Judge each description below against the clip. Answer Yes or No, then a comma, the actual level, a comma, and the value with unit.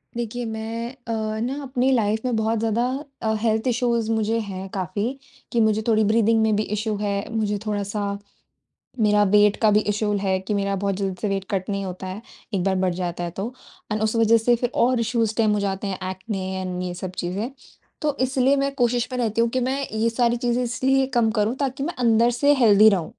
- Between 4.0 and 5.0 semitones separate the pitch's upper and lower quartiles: No, average, 2.8 semitones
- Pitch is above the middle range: Yes, high, 220 Hz